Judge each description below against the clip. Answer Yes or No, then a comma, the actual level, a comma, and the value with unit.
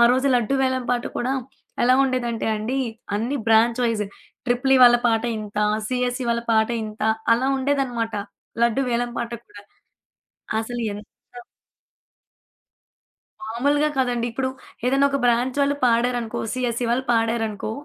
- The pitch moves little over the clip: Yes, narrow, 2.1 semitones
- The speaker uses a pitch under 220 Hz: No, high, 240 Hz